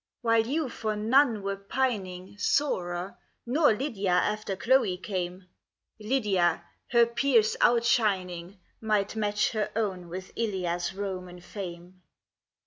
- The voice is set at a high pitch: Yes, high, 205 Hz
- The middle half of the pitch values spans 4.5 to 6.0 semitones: No, average, 4.0 semitones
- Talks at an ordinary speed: No, slow, 120 wpm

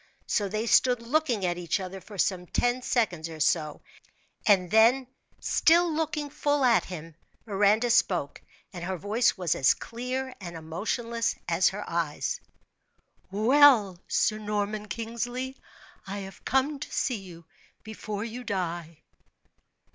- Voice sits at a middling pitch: No, high, 210 Hz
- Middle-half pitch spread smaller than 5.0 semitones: No, wide, 5.4 semitones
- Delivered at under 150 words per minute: Yes, average, 140 wpm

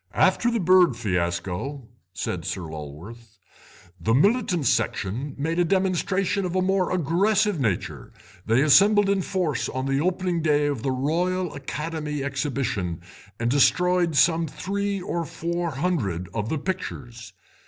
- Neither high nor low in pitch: Yes, medium, 150 Hz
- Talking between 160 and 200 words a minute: No, average, 140 wpm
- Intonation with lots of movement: Yes, wide, 7.4 semitones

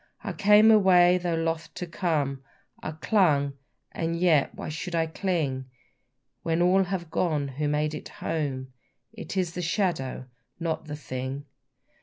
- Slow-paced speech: No, average, 150 wpm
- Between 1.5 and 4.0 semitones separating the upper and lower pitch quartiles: Yes, average, 3.5 semitones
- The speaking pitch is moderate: Yes, medium, 165 Hz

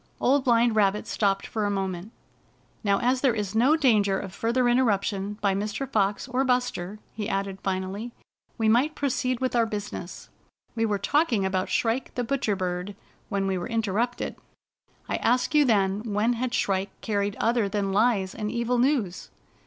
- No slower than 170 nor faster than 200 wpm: Yes, average, 175 wpm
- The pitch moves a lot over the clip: No, average, 3.7 semitones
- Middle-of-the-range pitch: No, high, 215 Hz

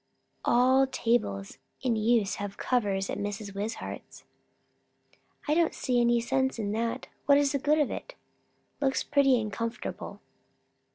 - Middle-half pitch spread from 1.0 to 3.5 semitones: No, average, 4.1 semitones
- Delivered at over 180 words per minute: No, slow, 135 wpm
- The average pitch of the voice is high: Yes, high, 240 Hz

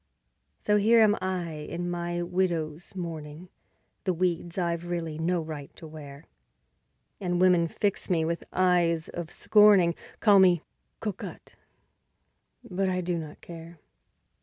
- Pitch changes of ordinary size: No, narrow, 2.1 semitones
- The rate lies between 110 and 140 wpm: Yes, slow, 135 wpm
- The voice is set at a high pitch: No, medium, 175 Hz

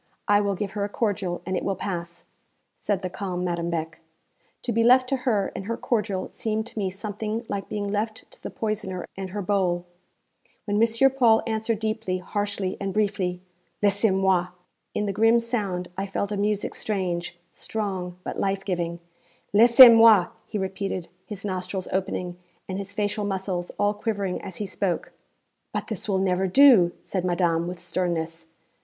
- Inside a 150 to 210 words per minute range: Yes, average, 175 wpm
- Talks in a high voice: Yes, high, 195 Hz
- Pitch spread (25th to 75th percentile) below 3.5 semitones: Yes, average, 2.8 semitones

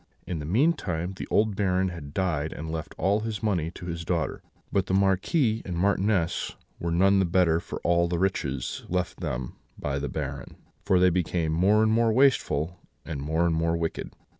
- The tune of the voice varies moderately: Yes, average, 3.1 semitones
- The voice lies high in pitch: No, very low, 90 Hz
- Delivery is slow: No, average, 190 wpm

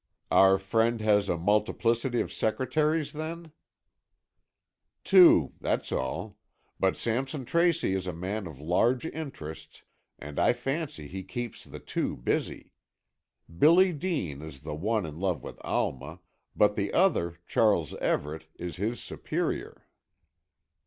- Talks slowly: Yes, slow, 130 wpm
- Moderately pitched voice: No, low, 105 Hz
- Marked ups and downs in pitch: Yes, wide, 8.2 semitones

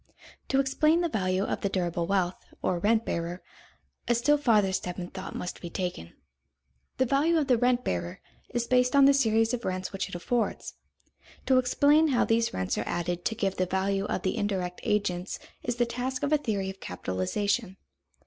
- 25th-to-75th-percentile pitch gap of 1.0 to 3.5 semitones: No, average, 5.3 semitones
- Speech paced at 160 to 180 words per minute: No, average, 195 wpm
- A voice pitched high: Yes, high, 210 Hz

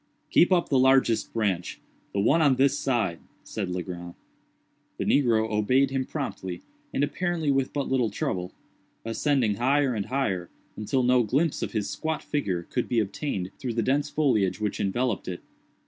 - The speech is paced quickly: No, average, 165 wpm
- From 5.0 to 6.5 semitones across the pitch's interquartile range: Yes, average, 5.3 semitones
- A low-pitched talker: Yes, low, 125 Hz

